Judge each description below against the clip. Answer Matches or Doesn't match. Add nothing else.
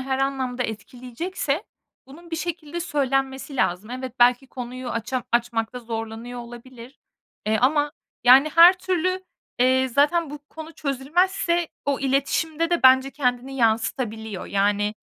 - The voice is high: Matches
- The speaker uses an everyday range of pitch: Matches